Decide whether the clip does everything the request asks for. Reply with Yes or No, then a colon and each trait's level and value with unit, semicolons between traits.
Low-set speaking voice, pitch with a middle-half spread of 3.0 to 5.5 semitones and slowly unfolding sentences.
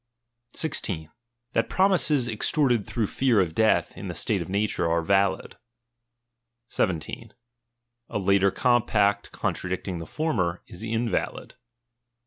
Yes: low, 105 Hz; average, 4.4 semitones; slow, 115 wpm